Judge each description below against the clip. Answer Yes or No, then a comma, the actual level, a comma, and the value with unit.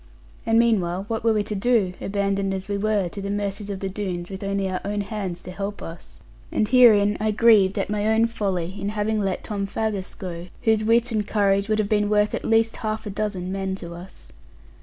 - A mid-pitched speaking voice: No, high, 205 Hz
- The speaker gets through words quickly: Yes, fast, 225 wpm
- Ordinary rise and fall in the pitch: No, narrow, 1.9 semitones